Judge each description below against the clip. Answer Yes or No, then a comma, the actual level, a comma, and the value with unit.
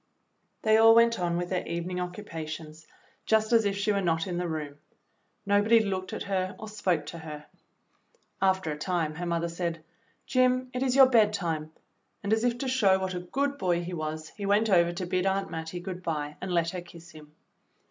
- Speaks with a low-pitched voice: No, medium, 180 Hz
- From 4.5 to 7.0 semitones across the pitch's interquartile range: No, average, 4.0 semitones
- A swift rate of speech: Yes, fast, 210 wpm